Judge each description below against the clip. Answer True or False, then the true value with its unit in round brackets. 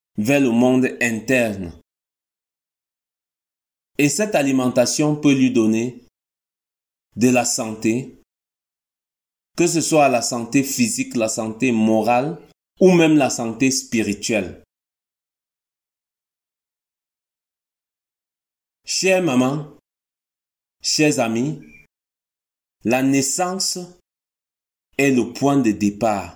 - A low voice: True (120 Hz)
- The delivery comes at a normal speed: False (85 wpm)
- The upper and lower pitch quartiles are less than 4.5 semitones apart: False (5.4 semitones)